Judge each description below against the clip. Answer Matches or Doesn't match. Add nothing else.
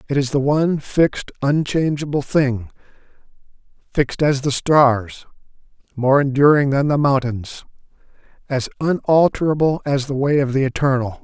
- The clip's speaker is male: Matches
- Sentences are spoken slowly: Matches